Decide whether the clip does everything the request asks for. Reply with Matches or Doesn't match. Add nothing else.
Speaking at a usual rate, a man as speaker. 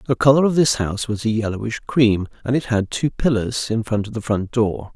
Doesn't match